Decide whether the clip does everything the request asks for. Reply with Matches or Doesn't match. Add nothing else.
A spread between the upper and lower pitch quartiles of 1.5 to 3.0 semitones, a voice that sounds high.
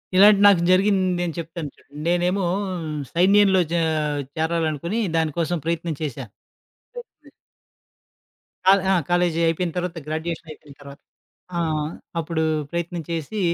Doesn't match